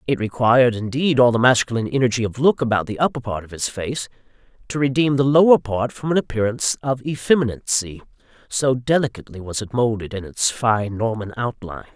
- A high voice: No, low, 120 Hz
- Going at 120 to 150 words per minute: No, average, 180 wpm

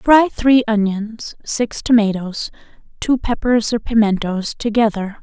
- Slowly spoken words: Yes, slow, 115 wpm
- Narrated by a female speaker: Yes, female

